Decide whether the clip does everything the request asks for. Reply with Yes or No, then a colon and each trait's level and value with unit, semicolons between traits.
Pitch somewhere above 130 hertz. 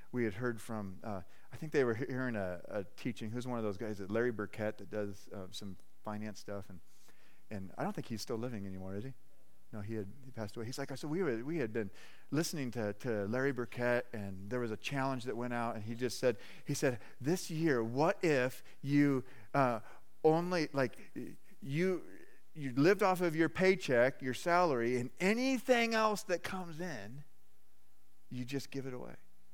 No: low, 125 Hz